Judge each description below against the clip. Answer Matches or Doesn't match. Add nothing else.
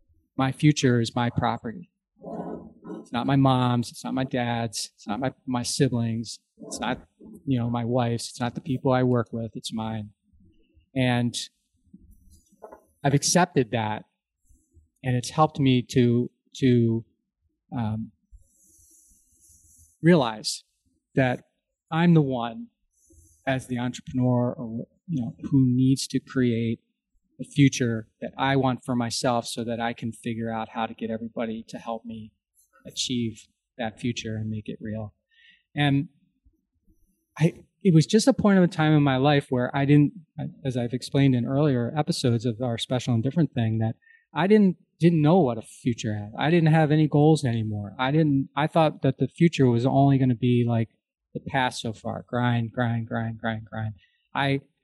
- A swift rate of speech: Doesn't match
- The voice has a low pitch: Matches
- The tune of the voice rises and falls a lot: Doesn't match